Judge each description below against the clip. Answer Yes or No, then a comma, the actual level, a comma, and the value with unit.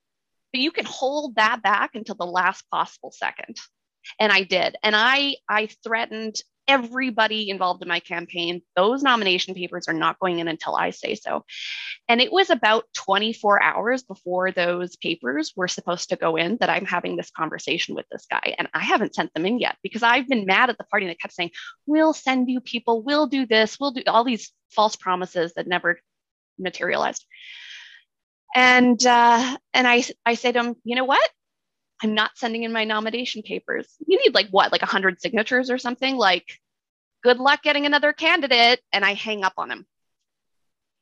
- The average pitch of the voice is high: Yes, high, 225 Hz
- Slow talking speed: No, average, 185 wpm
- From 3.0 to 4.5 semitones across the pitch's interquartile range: No, average, 5.1 semitones